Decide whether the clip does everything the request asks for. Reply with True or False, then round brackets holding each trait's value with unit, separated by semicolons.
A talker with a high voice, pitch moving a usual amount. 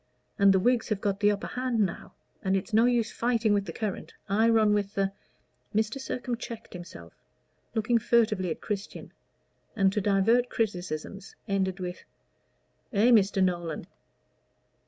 True (205 Hz; 3.0 semitones)